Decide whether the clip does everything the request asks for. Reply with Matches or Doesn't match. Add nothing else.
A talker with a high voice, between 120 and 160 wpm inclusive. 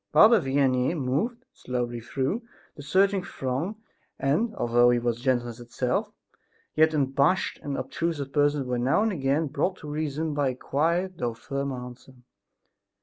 Doesn't match